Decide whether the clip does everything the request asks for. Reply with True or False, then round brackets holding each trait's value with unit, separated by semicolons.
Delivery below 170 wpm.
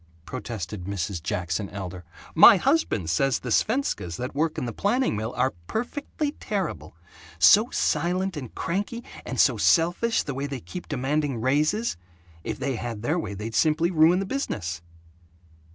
True (155 wpm)